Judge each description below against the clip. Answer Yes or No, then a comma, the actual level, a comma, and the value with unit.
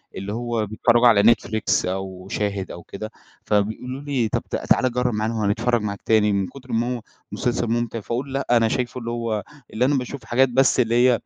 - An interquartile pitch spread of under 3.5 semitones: Yes, average, 2.8 semitones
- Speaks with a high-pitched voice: No, low, 115 Hz